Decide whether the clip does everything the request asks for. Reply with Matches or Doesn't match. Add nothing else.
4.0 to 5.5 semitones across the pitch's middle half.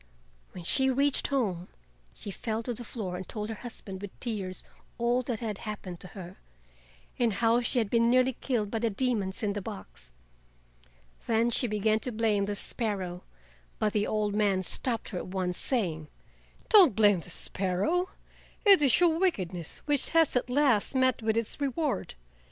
Matches